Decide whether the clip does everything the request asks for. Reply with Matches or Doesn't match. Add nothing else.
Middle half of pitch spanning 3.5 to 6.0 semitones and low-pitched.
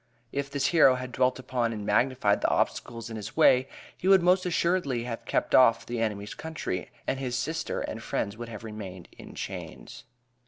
Matches